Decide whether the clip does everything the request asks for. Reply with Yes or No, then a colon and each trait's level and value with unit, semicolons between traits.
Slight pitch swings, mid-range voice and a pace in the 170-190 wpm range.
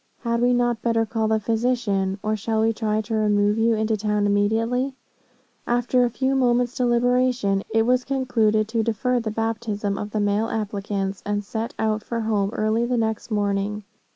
No: narrow, 2.3 semitones; high, 220 Hz; average, 180 wpm